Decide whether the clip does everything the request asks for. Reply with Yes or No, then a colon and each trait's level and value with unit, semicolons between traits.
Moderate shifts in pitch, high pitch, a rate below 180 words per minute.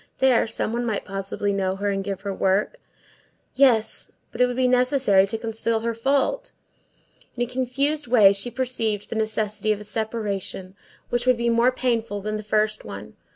No: average, 3.5 semitones; high, 220 Hz; average, 185 wpm